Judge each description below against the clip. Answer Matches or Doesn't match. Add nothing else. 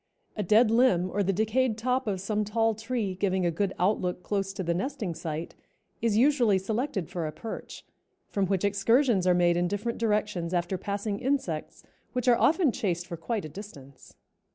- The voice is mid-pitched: Doesn't match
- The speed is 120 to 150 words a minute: Doesn't match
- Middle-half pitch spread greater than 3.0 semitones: Matches